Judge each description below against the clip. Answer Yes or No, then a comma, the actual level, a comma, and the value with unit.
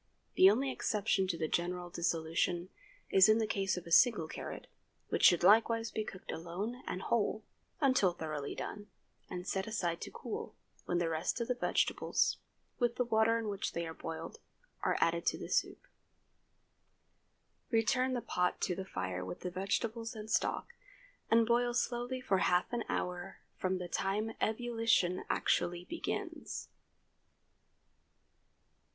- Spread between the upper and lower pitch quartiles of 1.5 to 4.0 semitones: No, average, 4.7 semitones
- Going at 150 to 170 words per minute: Yes, average, 155 wpm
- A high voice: Yes, high, 195 Hz